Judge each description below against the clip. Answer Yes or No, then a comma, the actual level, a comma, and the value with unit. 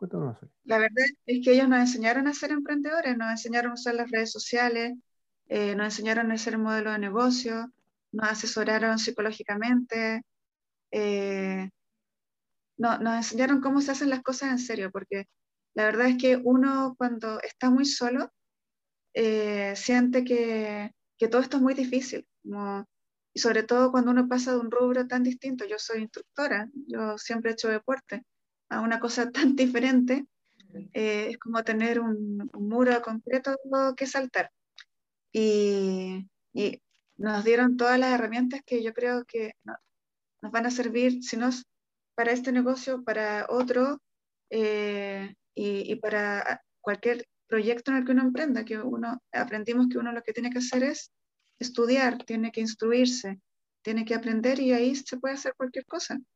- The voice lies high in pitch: Yes, high, 235 Hz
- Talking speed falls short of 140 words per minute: No, average, 165 wpm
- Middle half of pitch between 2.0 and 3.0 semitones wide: Yes, narrow, 2.6 semitones